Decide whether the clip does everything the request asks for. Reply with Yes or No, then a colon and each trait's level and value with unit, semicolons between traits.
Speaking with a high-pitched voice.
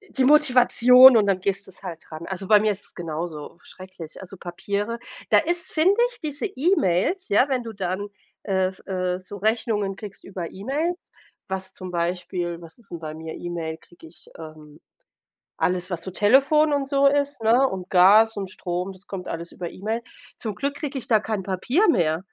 Yes: high, 195 Hz